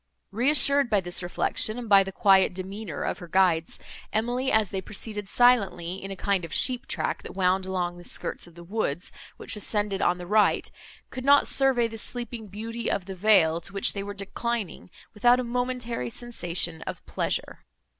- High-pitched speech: Yes, high, 200 Hz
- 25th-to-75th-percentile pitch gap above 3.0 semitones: Yes, average, 4.5 semitones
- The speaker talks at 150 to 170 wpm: No, average, 185 wpm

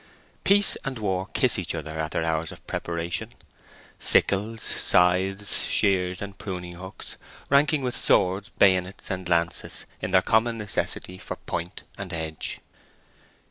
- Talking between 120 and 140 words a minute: Yes, slow, 135 wpm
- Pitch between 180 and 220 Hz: No, very low, 95 Hz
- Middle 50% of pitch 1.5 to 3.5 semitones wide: Yes, average, 2.8 semitones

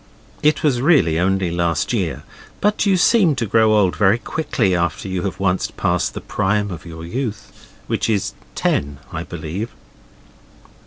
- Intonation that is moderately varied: No, wide, 5.9 semitones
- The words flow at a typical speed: Yes, average, 165 wpm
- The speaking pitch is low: Yes, low, 100 Hz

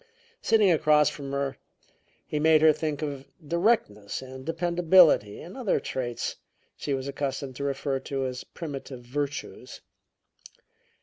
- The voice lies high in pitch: No, medium, 140 Hz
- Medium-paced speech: No, slow, 130 wpm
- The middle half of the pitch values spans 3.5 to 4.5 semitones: No, average, 3.1 semitones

